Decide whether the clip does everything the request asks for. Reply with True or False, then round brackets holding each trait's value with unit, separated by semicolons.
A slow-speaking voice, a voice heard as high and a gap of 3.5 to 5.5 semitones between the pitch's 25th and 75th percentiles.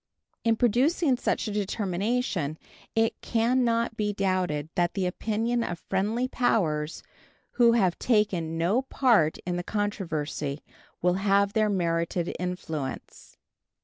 True (125 wpm; 200 Hz; 4.9 semitones)